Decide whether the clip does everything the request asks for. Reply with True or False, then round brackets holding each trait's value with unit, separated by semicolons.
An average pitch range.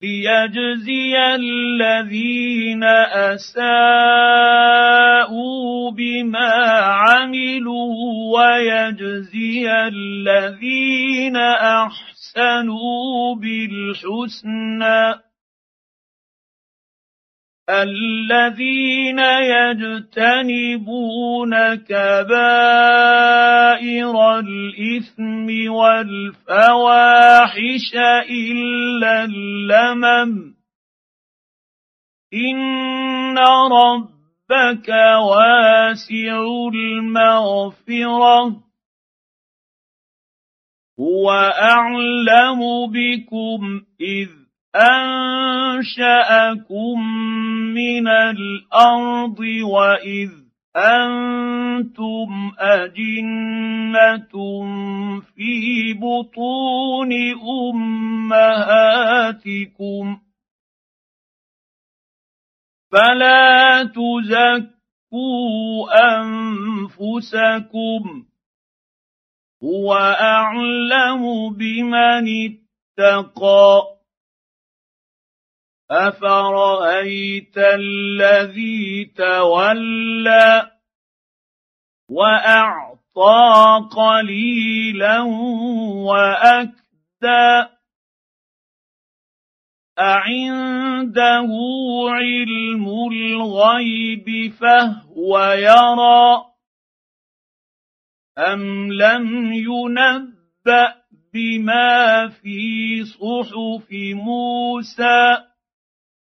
False (1.8 semitones)